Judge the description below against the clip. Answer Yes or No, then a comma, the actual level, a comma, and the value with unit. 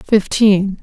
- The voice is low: No, high, 200 Hz